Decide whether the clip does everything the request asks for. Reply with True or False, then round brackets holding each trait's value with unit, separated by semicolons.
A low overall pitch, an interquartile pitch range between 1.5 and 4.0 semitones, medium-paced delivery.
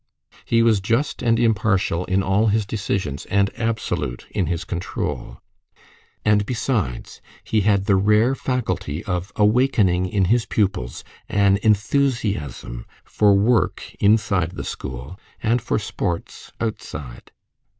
False (100 Hz; 3.6 semitones; 125 wpm)